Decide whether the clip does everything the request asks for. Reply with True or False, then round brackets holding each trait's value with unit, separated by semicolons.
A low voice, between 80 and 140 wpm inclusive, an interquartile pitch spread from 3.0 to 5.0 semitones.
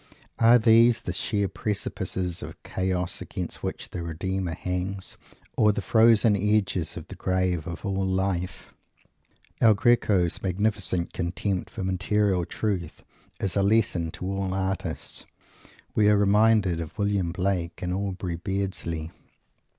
False (95 Hz; 135 wpm; 2.4 semitones)